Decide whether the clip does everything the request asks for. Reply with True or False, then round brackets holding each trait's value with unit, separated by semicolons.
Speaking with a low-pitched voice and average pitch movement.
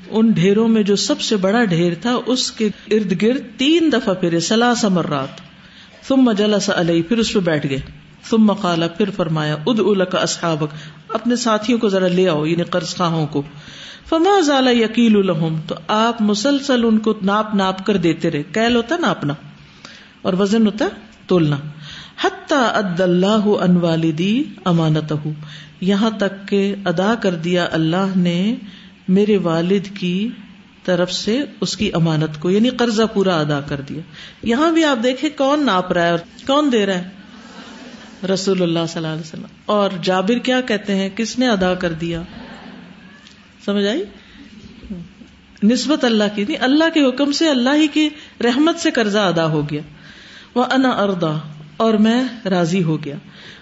False (200 Hz; 4.9 semitones)